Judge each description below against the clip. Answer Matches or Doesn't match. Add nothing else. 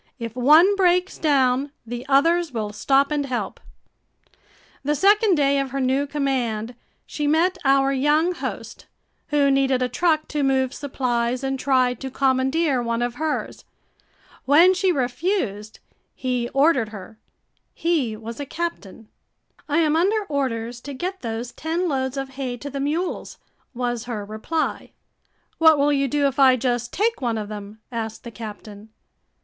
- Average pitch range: Matches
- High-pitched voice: Matches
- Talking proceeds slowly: Doesn't match